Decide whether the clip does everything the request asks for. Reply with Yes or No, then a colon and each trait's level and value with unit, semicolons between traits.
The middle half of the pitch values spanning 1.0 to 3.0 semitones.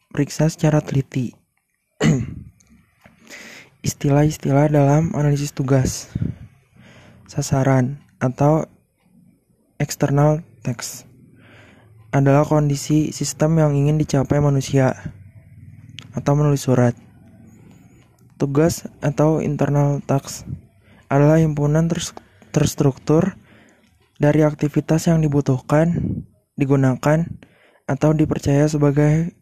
Yes: average, 2.7 semitones